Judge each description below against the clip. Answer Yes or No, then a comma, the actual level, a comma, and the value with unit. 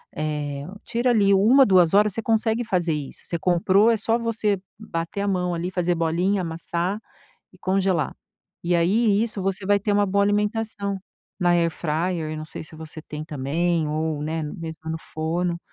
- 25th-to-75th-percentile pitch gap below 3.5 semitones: No, average, 4.1 semitones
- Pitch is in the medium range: Yes, medium, 180 Hz